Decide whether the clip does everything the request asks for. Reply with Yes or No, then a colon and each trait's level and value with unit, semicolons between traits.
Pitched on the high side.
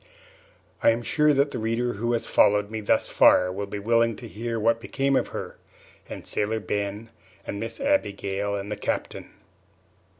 No: low, 110 Hz